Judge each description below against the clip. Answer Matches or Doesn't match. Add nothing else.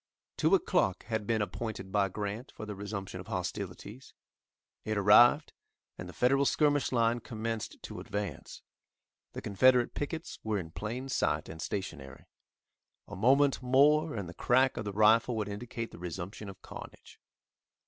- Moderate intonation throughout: Matches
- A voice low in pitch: Matches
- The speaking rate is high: Doesn't match